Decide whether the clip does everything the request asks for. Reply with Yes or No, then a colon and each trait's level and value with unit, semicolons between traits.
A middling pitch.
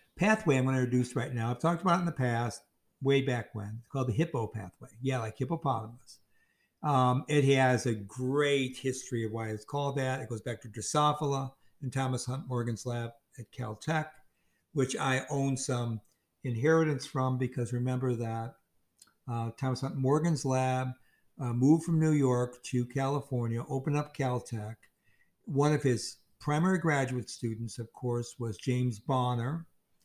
No: low, 130 Hz